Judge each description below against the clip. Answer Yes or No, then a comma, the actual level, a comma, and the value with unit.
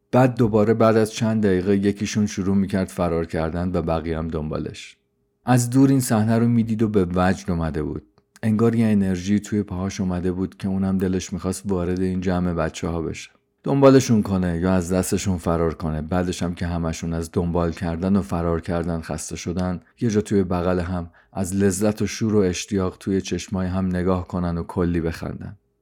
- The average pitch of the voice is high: No, very low, 95 Hz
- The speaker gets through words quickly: Yes, fast, 190 wpm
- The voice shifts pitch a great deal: No, average, 3.0 semitones